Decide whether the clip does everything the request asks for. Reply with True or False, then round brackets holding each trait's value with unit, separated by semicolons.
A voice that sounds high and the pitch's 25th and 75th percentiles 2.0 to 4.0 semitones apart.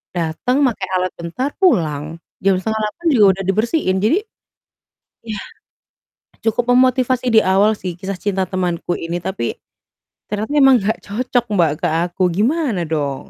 False (205 Hz; 5.4 semitones)